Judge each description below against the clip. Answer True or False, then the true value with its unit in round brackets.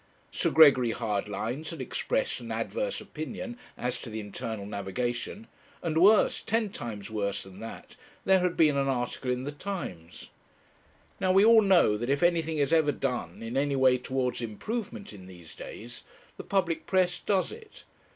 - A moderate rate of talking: True (170 wpm)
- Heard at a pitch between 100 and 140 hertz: True (135 Hz)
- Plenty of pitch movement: True (8.5 semitones)